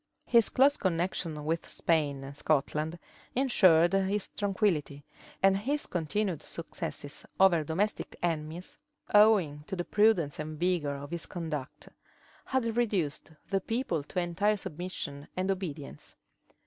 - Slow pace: Yes, slow, 125 wpm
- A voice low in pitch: No, medium, 175 Hz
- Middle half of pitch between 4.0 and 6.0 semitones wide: Yes, average, 4.8 semitones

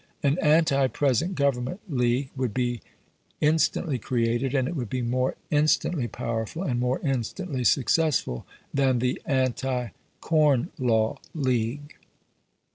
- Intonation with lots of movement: No, average, 3.2 semitones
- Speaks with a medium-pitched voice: No, low, 130 Hz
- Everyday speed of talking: No, slow, 120 wpm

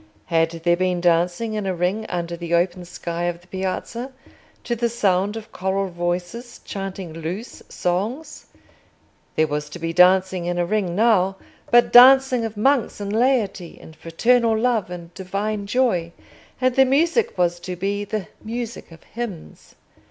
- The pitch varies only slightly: No, average, 4.8 semitones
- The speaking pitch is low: No, high, 190 Hz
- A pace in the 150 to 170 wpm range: Yes, average, 160 wpm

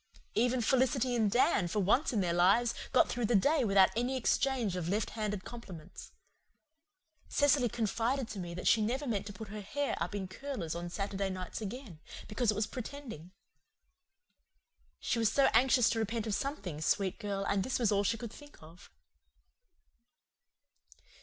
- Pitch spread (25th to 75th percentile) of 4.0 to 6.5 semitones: Yes, average, 4.3 semitones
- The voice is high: Yes, high, 215 Hz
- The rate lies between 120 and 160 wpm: No, average, 170 wpm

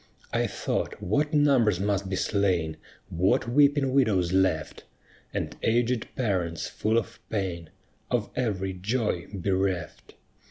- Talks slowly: Yes, slow, 120 wpm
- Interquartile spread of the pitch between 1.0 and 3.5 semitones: No, average, 4.7 semitones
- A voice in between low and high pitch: No, low, 100 Hz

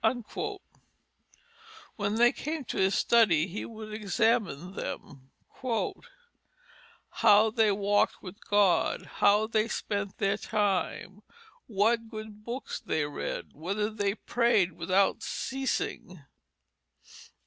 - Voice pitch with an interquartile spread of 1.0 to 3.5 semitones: Yes, narrow, 2.6 semitones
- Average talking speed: No, slow, 105 wpm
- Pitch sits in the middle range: No, high, 205 Hz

